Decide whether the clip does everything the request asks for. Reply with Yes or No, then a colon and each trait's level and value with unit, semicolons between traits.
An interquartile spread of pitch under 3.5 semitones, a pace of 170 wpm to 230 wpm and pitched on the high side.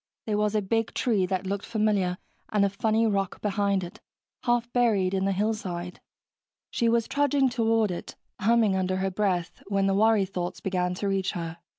Yes: average, 2.9 semitones; average, 185 wpm; high, 200 Hz